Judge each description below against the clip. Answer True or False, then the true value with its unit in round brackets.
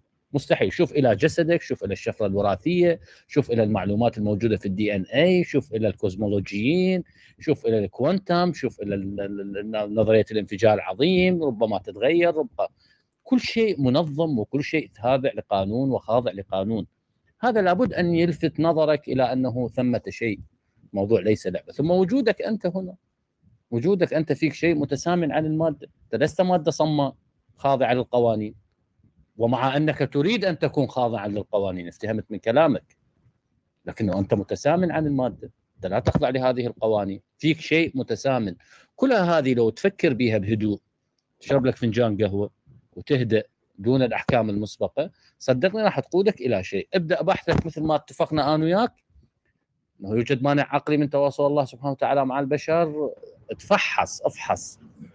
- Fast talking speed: True (145 wpm)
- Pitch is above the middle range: False (135 Hz)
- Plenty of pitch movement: True (7.1 semitones)